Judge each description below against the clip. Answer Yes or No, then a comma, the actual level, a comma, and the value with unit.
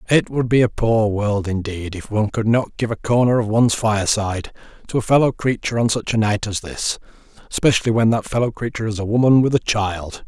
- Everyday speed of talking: No, fast, 220 wpm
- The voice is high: No, low, 110 Hz